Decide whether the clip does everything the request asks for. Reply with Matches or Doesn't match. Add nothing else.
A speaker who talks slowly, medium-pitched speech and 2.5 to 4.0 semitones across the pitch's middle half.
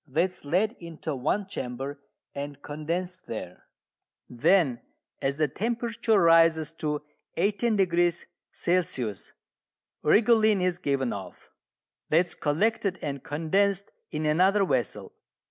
Doesn't match